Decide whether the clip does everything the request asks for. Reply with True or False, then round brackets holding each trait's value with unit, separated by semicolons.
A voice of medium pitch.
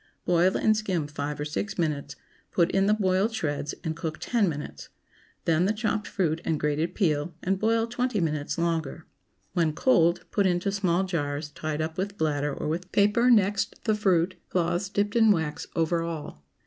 True (175 Hz)